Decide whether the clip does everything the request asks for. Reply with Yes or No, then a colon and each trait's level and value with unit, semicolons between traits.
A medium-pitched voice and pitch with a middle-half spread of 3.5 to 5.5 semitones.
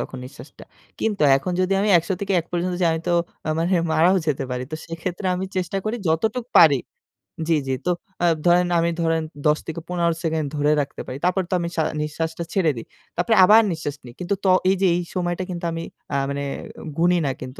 No: medium, 170 Hz; average, 2.9 semitones